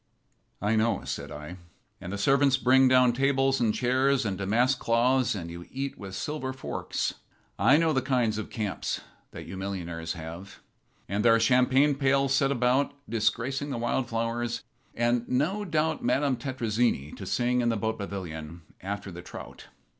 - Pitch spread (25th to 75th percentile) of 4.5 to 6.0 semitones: Yes, average, 4.8 semitones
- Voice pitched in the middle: No, low, 120 Hz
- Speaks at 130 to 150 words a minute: No, average, 170 wpm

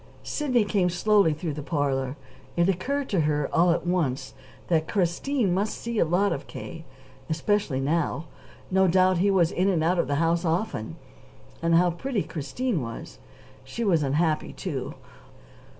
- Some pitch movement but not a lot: Yes, average, 4.1 semitones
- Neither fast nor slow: Yes, average, 165 wpm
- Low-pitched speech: No, medium, 175 Hz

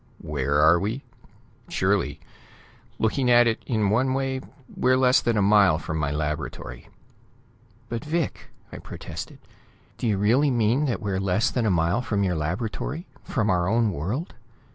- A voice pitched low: Yes, low, 110 Hz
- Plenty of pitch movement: Yes, wide, 6.0 semitones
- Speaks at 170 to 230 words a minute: No, average, 160 wpm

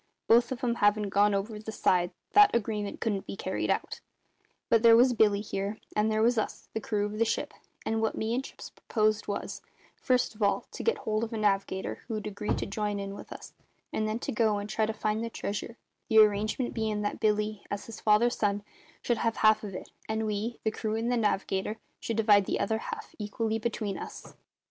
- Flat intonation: Yes, narrow, 1.5 semitones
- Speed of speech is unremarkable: No, fast, 215 wpm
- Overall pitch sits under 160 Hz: No, high, 215 Hz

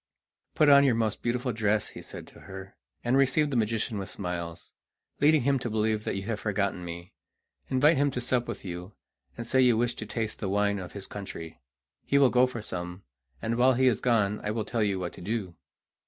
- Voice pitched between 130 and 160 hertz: No, low, 110 Hz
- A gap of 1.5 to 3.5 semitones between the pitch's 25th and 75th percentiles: No, average, 4.2 semitones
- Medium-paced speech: No, fast, 220 wpm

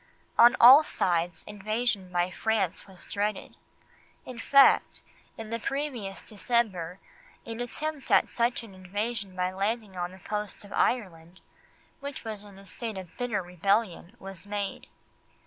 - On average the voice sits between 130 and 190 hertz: No, high, 205 Hz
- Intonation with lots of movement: No, average, 3.9 semitones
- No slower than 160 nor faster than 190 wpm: No, average, 145 wpm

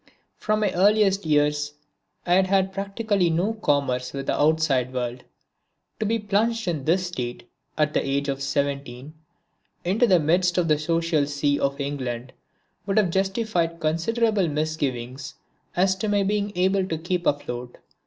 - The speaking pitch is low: No, medium, 165 Hz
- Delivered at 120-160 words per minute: Yes, average, 155 wpm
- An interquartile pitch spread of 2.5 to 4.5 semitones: No, wide, 5.5 semitones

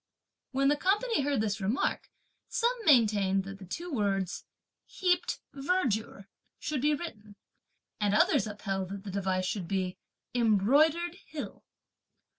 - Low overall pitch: No, high, 220 Hz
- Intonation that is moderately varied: No, wide, 7.2 semitones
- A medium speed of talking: No, slow, 130 wpm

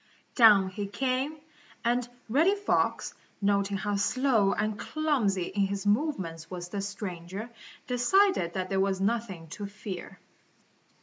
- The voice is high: Yes, high, 205 Hz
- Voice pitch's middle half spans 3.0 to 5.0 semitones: Yes, average, 4.2 semitones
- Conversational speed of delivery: No, slow, 130 wpm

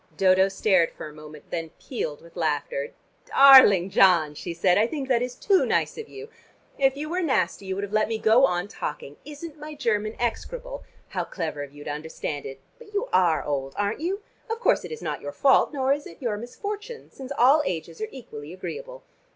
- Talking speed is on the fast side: Yes, fast, 210 wpm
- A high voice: Yes, high, 215 Hz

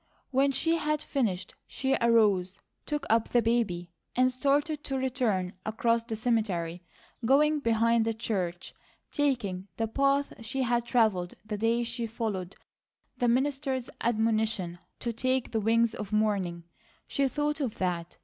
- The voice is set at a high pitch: Yes, high, 230 Hz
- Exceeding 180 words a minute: No, average, 145 wpm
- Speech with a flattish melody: No, average, 3.9 semitones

